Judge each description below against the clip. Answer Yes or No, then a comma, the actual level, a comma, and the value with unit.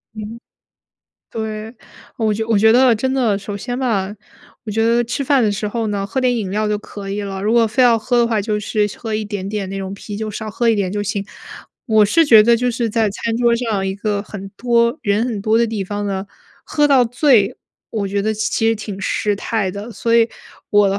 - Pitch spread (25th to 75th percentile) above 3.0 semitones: No, narrow, 2.4 semitones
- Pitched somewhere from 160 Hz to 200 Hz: No, high, 215 Hz